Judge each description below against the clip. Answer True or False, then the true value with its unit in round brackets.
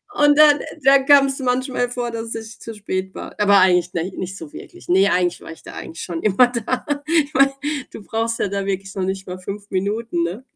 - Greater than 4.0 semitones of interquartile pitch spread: True (5.1 semitones)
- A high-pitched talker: True (210 Hz)